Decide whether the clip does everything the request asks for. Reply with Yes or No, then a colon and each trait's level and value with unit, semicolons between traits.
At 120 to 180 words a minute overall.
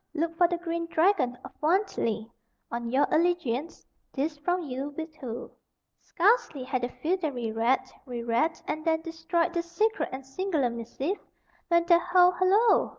Yes: average, 155 wpm